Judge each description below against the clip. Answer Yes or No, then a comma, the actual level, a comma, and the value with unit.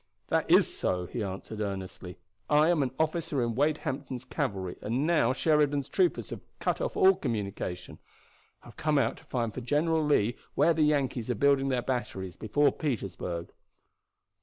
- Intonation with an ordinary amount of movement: No, wide, 6.3 semitones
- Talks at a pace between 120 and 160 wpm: No, average, 170 wpm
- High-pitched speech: No, low, 130 Hz